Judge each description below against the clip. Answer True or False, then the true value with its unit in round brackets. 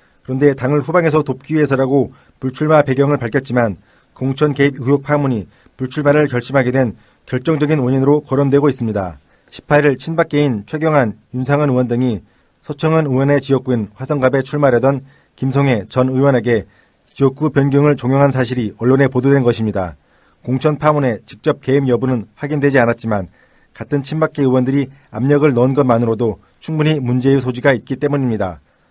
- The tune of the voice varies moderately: True (3.2 semitones)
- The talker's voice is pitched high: False (135 Hz)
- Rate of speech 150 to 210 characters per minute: False (370 characters per minute)